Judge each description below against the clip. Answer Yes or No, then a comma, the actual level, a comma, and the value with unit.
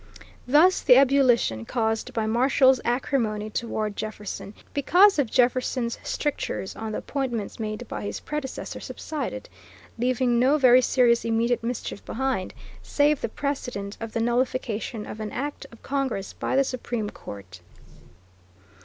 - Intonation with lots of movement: No, average, 3.5 semitones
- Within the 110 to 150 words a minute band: Yes, slow, 135 wpm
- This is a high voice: Yes, high, 245 Hz